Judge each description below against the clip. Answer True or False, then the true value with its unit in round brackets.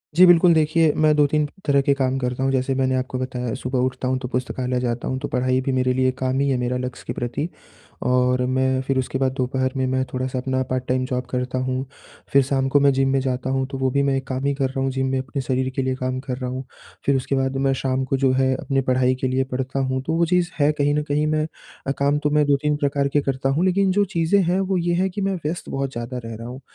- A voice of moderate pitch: False (130 Hz)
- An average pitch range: False (1.7 semitones)